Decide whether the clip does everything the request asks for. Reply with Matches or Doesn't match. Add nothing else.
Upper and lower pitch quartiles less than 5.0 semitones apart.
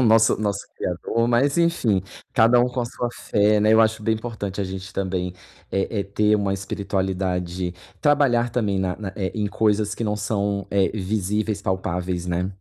Matches